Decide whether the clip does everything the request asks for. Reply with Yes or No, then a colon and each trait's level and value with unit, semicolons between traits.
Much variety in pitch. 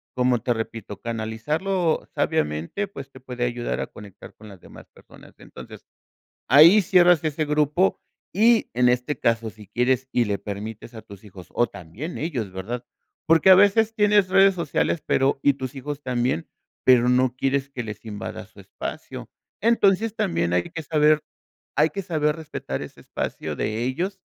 Yes: wide, 6.6 semitones